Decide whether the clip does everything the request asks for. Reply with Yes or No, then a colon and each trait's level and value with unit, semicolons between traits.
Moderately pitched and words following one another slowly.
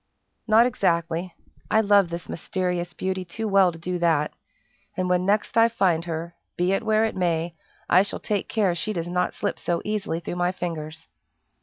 No: medium, 180 Hz; average, 185 wpm